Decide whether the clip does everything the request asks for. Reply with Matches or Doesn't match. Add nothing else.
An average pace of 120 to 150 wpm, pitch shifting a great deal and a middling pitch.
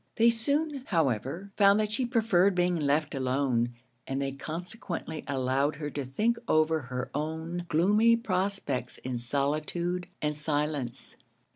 Matches